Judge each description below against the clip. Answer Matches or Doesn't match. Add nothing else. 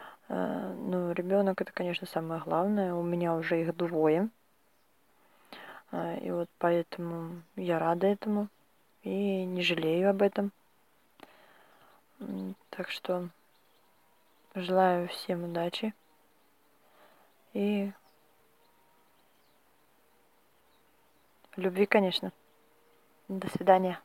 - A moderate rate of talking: Doesn't match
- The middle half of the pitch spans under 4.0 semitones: Matches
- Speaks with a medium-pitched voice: Matches